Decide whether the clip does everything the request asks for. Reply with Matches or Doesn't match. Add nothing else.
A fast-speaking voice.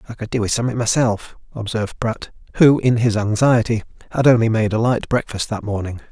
Doesn't match